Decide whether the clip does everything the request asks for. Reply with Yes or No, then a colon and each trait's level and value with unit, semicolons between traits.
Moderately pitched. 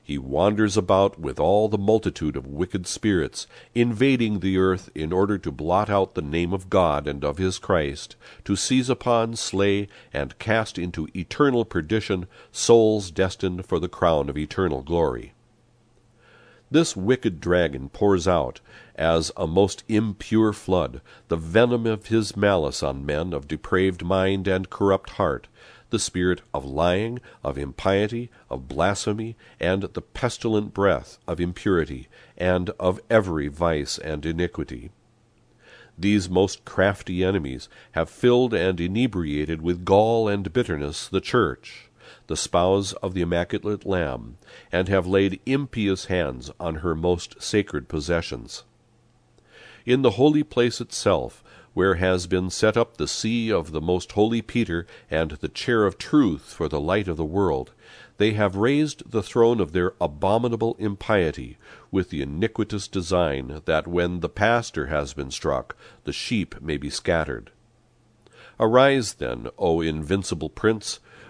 No: very low, 95 Hz